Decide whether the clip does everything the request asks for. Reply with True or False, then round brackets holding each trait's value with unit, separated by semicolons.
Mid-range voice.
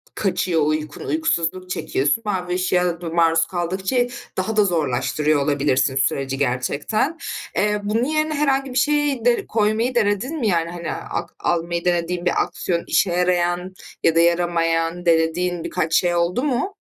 True (175 Hz)